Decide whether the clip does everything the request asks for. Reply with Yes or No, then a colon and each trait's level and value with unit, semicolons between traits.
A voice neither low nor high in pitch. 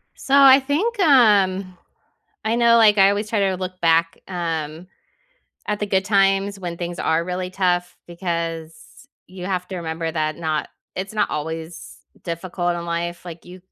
Yes: medium, 180 Hz